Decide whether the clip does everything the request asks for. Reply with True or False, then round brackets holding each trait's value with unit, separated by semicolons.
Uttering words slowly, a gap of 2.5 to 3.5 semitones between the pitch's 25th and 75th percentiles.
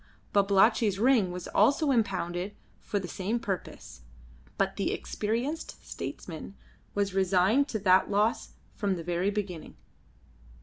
True (125 wpm; 3.1 semitones)